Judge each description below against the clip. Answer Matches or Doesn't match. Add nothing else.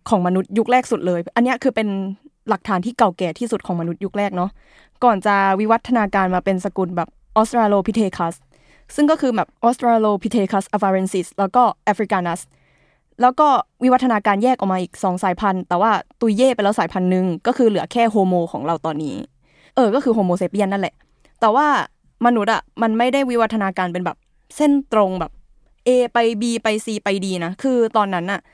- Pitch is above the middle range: Matches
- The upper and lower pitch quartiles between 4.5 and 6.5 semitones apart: Doesn't match